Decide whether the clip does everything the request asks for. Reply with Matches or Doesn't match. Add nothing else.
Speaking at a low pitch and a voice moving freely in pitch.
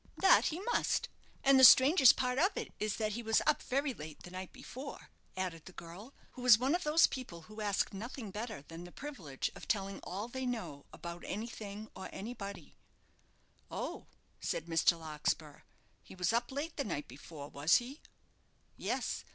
Doesn't match